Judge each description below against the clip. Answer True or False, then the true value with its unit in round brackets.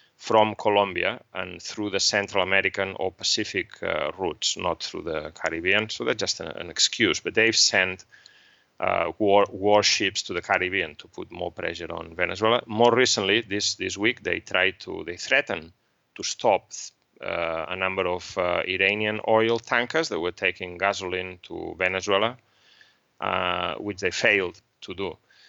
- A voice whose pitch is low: True (100 Hz)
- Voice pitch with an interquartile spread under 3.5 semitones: True (2.5 semitones)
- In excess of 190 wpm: False (160 wpm)